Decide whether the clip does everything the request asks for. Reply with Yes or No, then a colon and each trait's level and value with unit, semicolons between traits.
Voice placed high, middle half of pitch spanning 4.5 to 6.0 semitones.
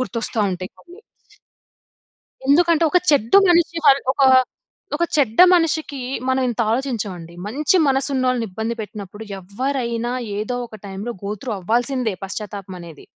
Yes: high, 240 Hz; average, 5.1 semitones